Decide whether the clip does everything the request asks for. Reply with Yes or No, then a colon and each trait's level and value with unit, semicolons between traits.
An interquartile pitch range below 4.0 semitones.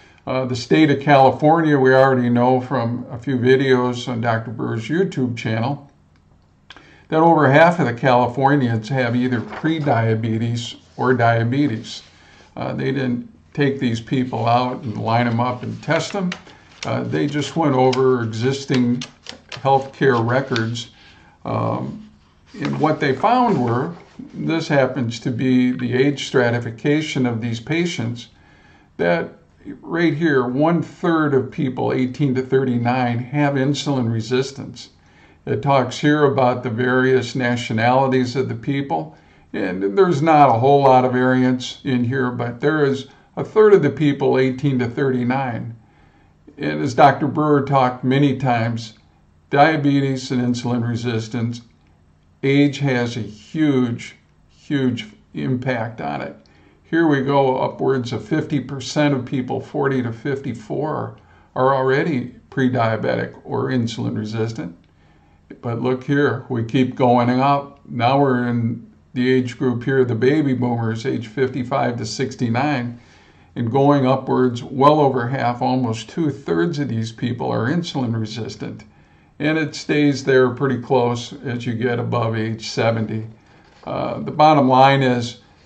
Yes: average, 2.9 semitones